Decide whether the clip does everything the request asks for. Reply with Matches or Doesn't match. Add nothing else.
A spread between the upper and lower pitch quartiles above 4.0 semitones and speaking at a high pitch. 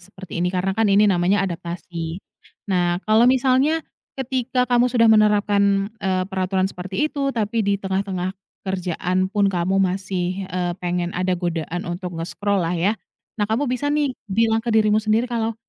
Doesn't match